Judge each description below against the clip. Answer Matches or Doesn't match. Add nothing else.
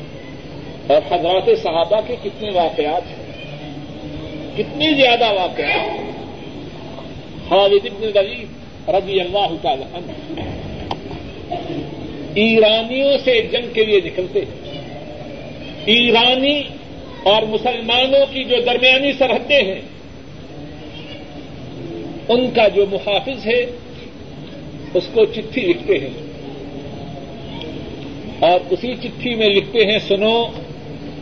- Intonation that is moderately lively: Doesn't match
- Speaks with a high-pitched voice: Matches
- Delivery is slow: Matches